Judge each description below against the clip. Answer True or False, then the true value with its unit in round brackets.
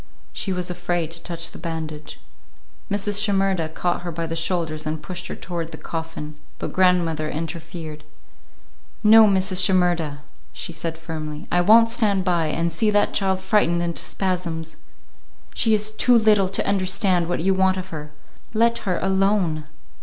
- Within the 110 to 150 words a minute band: False (160 wpm)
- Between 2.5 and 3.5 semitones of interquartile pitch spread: True (3.0 semitones)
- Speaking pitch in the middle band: True (175 Hz)